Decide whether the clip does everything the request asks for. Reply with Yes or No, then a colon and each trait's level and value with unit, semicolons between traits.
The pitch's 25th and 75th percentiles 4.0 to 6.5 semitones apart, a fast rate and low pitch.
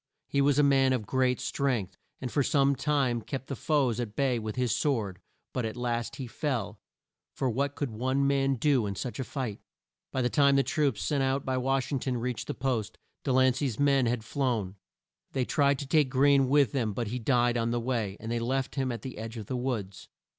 No: average, 2.8 semitones; fast, 225 wpm; low, 130 Hz